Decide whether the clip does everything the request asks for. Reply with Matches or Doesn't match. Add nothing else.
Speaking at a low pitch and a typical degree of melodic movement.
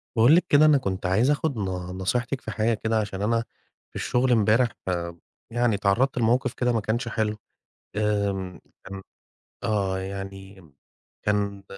Matches